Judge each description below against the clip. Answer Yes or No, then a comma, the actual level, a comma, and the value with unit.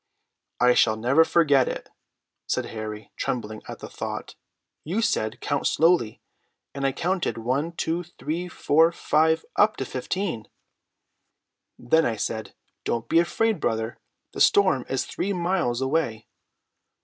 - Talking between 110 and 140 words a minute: Yes, slow, 135 wpm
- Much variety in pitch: Yes, wide, 6.4 semitones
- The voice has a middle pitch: Yes, medium, 145 Hz